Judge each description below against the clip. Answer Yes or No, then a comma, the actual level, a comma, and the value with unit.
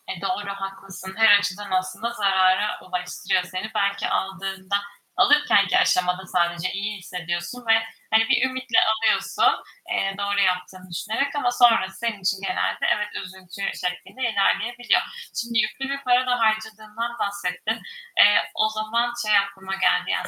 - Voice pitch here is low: No, high, 200 Hz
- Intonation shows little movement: No, average, 3.2 semitones